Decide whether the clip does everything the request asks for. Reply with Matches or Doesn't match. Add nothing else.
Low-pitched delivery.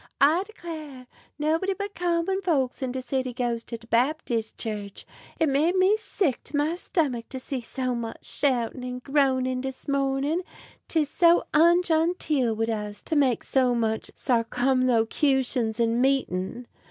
Doesn't match